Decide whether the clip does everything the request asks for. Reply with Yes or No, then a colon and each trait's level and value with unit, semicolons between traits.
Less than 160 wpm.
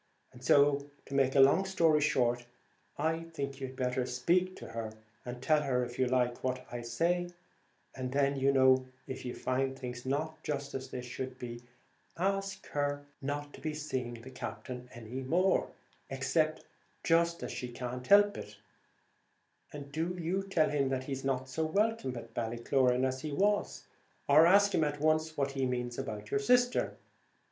No: average, 175 wpm